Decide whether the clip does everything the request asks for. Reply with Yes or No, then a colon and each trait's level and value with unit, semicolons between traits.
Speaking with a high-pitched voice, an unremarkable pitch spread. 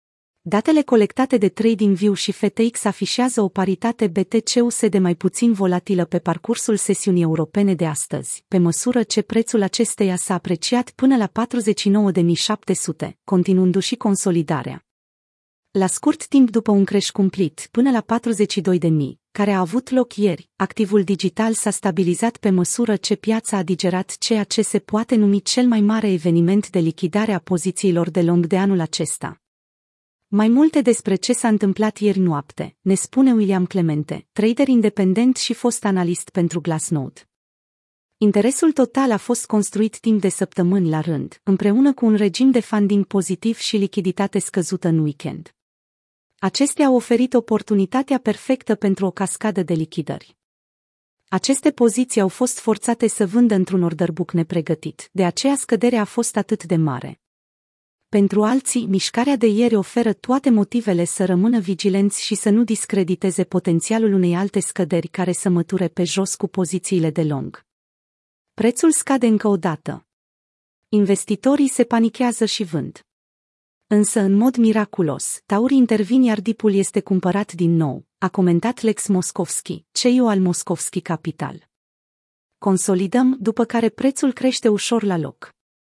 Yes: high, 200 Hz; average, 3.9 semitones